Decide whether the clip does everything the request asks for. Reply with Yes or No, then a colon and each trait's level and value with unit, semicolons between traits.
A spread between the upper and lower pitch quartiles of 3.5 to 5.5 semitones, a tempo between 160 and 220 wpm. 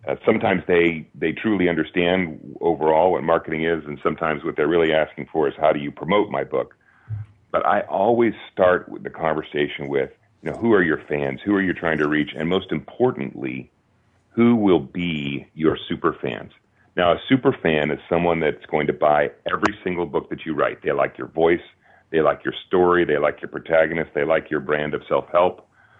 No: average, 3.1 semitones; fast, 205 wpm